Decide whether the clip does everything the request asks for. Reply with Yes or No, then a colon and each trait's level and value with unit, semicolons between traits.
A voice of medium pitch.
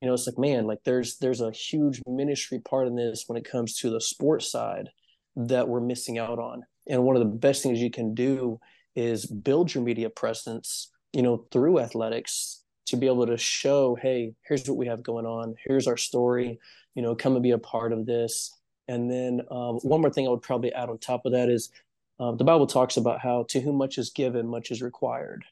No: low, 125 Hz